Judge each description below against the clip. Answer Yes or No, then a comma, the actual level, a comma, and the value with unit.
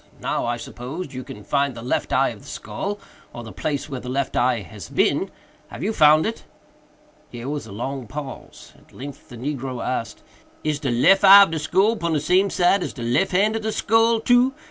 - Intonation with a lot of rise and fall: Yes, wide, 7.7 semitones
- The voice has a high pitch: No, medium, 145 Hz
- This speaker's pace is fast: Yes, fast, 220 wpm